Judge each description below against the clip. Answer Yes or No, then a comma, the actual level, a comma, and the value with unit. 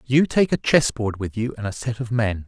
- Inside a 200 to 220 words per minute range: No, fast, 265 wpm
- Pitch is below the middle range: Yes, low, 115 Hz